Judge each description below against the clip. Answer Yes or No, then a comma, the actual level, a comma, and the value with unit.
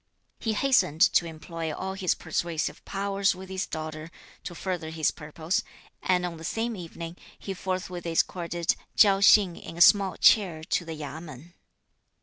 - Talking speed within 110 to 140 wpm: No, average, 155 wpm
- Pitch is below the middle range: No, medium, 175 Hz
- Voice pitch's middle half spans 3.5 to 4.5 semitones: No, average, 2.9 semitones